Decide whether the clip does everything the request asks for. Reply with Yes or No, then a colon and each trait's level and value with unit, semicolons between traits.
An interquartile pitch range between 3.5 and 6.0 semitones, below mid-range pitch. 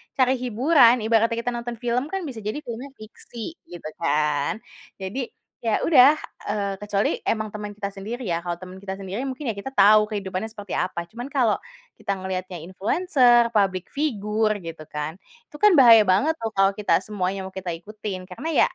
No: average, 4.2 semitones; high, 215 Hz